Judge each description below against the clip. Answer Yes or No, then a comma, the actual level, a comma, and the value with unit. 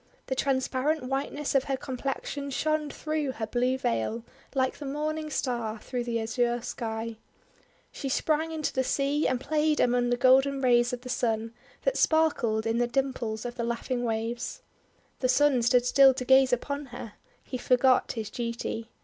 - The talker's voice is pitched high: Yes, very high, 255 Hz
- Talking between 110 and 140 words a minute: No, average, 170 wpm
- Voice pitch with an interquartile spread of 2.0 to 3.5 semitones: Yes, average, 2.7 semitones